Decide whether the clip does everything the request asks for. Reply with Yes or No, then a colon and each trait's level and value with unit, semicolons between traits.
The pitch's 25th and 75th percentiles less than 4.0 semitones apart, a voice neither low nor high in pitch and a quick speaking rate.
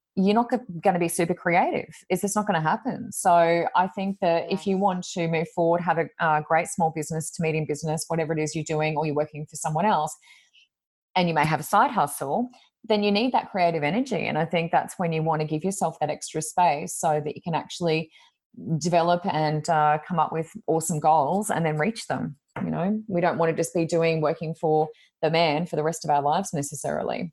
Yes: average, 2.9 semitones; medium, 165 Hz; fast, 235 wpm